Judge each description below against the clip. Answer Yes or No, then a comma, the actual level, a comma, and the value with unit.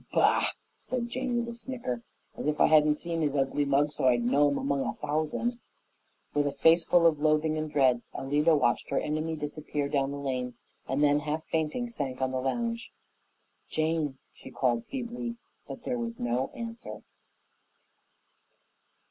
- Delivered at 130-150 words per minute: No, average, 170 wpm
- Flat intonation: No, average, 4.2 semitones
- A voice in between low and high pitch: Yes, medium, 150 Hz